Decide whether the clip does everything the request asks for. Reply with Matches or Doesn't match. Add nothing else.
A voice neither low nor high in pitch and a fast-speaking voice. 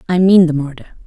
Matches